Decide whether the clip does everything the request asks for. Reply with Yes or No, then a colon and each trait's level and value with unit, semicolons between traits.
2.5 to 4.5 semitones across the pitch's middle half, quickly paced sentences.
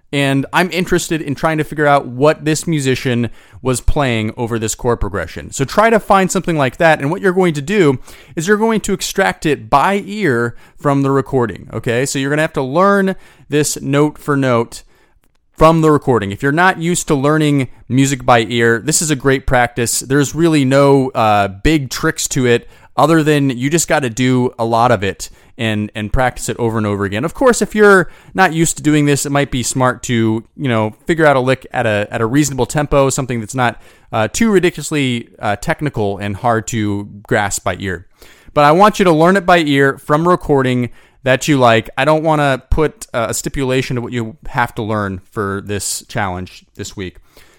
No: average, 5.0 semitones; fast, 215 wpm